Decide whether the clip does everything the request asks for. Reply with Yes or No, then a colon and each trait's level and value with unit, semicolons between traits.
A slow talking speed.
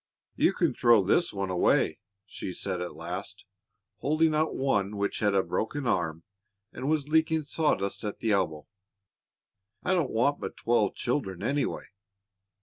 No: average, 150 wpm